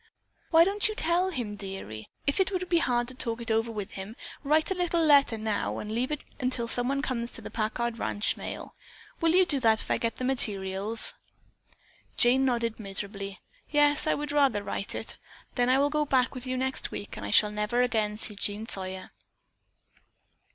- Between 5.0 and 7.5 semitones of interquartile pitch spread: Yes, wide, 5.4 semitones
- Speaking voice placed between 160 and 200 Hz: No, high, 245 Hz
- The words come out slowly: No, average, 200 wpm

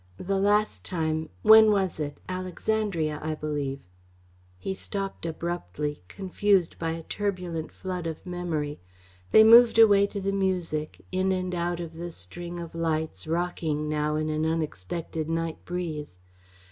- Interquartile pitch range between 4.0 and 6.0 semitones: No, average, 3.4 semitones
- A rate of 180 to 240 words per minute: No, average, 145 wpm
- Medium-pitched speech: Yes, medium, 170 Hz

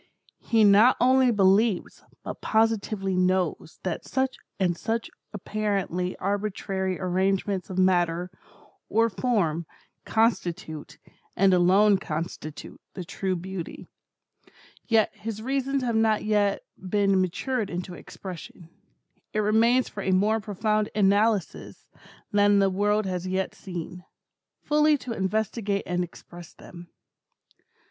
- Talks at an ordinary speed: No, slow, 115 wpm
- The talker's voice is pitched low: No, high, 200 Hz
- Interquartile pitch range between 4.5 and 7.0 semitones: No, average, 3.1 semitones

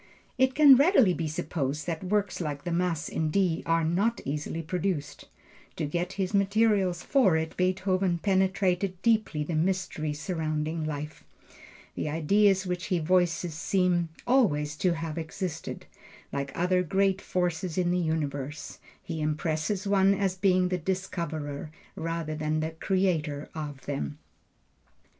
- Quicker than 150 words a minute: No, average, 140 wpm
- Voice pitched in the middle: Yes, medium, 175 Hz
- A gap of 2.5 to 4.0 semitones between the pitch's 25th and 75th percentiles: Yes, average, 3.5 semitones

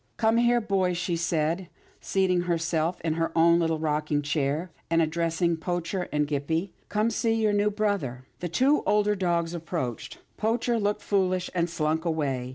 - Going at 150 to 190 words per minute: Yes, average, 170 wpm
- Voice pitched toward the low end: No, medium, 170 Hz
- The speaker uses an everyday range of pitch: Yes, average, 4.0 semitones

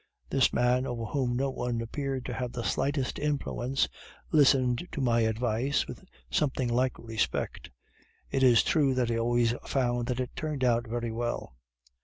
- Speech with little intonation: Yes, narrow, 2.1 semitones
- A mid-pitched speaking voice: No, low, 125 Hz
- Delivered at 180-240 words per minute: No, average, 165 wpm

